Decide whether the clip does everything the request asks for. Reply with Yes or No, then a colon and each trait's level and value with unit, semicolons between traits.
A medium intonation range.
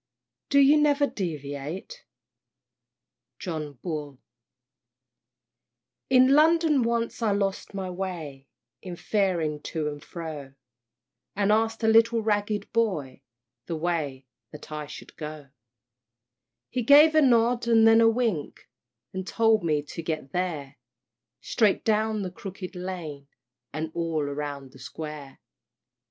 No: wide, 6.9 semitones